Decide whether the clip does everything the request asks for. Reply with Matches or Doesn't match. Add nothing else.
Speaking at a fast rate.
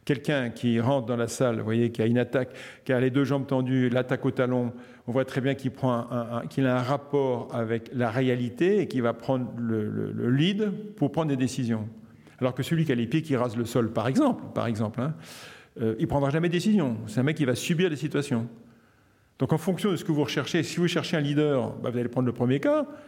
Matches